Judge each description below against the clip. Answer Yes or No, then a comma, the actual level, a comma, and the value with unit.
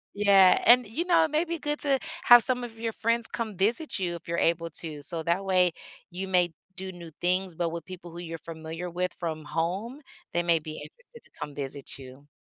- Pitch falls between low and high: Yes, medium, 180 Hz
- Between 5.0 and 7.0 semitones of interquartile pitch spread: Yes, wide, 5.6 semitones